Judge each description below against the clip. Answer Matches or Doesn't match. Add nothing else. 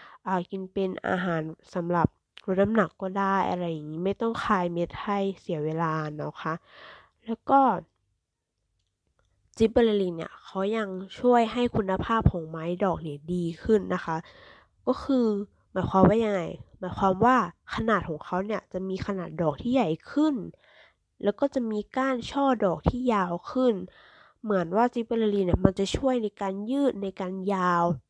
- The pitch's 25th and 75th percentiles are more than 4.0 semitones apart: Matches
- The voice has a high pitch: Matches